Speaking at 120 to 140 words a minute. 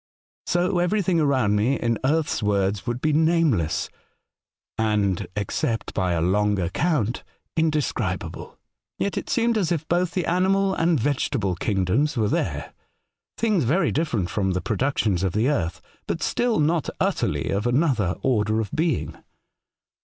No: average, 155 wpm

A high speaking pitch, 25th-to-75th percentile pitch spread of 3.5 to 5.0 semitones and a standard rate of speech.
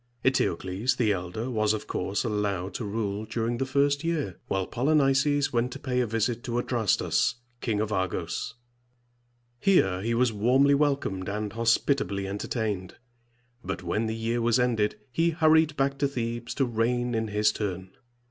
No: low, 115 Hz; average, 4.1 semitones; average, 165 wpm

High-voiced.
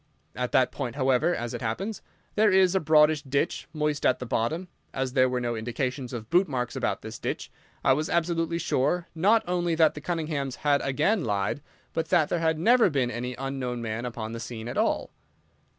No: medium, 140 Hz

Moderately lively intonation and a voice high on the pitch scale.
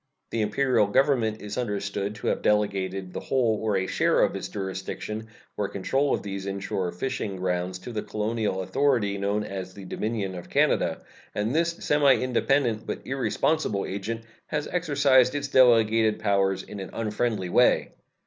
No: average, 4.3 semitones; low, 105 Hz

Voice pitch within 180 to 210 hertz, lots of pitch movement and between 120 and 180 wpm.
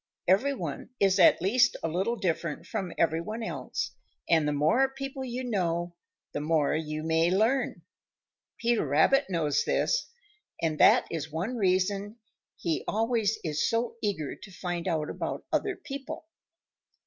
Yes: high, 190 Hz; wide, 6.5 semitones; average, 150 wpm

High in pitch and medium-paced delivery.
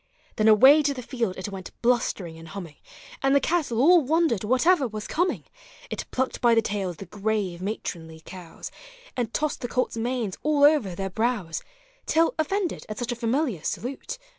Yes: high, 235 Hz; average, 180 wpm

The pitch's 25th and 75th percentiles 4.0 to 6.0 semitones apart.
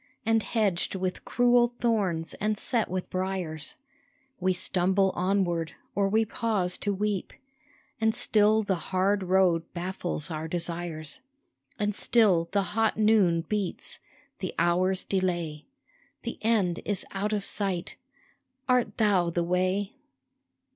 No: average, 3.3 semitones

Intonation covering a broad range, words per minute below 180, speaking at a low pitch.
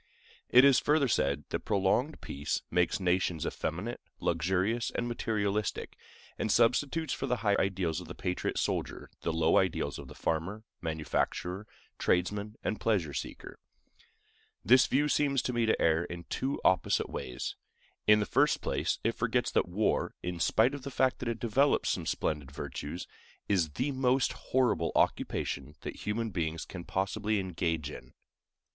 Yes: wide, 6.1 semitones; average, 160 wpm; low, 100 Hz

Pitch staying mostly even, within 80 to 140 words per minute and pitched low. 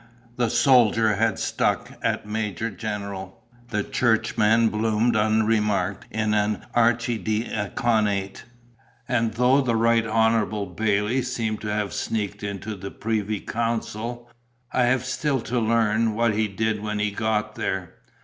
Yes: narrow, 1.7 semitones; slow, 135 wpm; low, 110 Hz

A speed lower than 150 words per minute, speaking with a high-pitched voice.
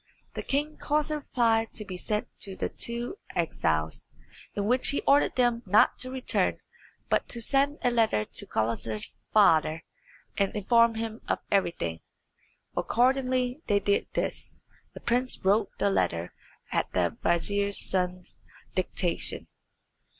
Yes: average, 140 wpm; high, 215 Hz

